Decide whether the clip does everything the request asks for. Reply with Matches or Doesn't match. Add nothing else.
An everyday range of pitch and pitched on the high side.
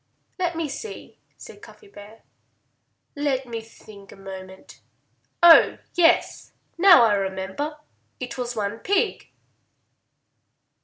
Doesn't match